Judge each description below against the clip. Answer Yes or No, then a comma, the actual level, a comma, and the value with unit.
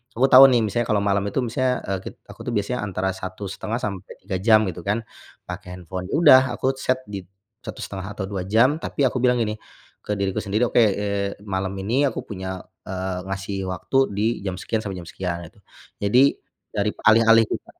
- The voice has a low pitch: Yes, low, 105 Hz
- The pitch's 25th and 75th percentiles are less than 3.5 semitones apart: No, average, 3.8 semitones